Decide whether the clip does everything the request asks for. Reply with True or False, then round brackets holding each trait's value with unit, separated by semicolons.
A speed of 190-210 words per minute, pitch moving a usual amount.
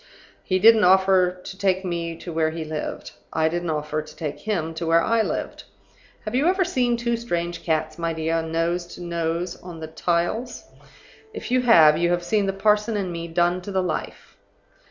True (195 wpm; 3.6 semitones)